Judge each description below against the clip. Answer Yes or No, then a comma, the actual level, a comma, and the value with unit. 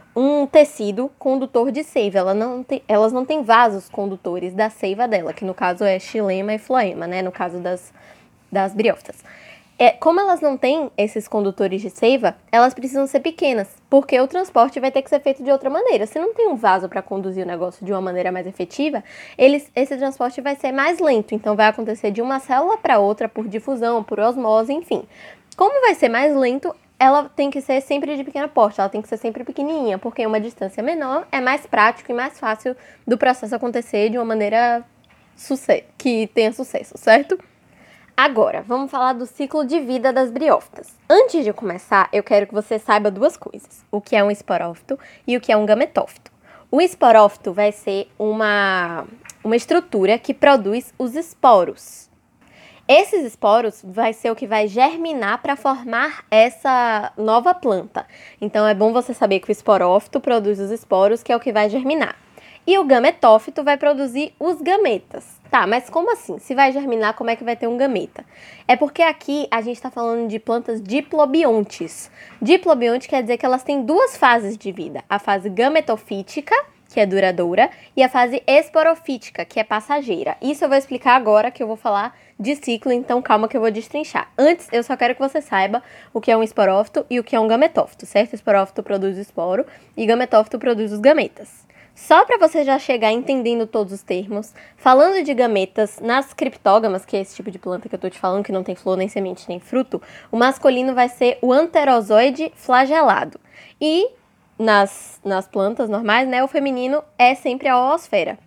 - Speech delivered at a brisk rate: Yes, fast, 195 wpm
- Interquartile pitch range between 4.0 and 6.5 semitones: Yes, average, 4.8 semitones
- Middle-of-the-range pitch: No, high, 240 Hz